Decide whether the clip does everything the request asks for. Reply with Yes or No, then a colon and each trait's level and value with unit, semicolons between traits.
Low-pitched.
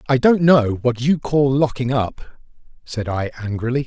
Yes: low, 130 Hz